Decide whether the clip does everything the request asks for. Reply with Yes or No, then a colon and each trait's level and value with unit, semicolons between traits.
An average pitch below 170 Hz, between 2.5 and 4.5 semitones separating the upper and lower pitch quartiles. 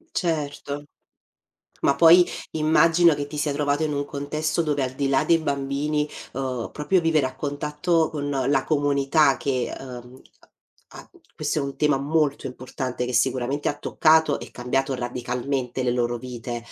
Yes: medium, 140 Hz; average, 2.8 semitones